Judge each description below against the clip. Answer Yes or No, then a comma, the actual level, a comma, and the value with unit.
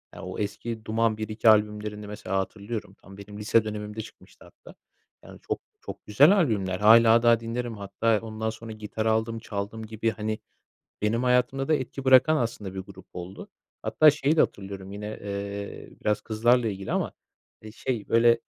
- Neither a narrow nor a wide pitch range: No, narrow, 2.2 semitones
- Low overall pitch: Yes, low, 110 Hz